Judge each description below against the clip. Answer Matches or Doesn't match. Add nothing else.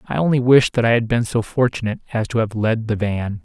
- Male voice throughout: Matches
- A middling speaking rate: Doesn't match